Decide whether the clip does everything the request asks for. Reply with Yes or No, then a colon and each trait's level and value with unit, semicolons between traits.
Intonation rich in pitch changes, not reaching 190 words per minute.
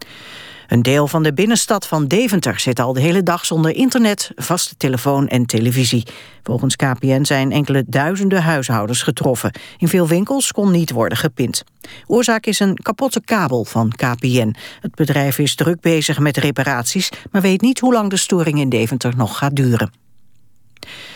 Yes: wide, 7.1 semitones; average, 165 wpm